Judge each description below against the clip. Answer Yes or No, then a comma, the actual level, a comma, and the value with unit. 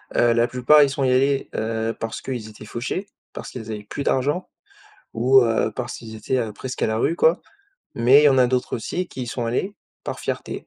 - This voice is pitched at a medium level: No, low, 125 Hz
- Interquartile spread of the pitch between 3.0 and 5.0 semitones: Yes, average, 3.3 semitones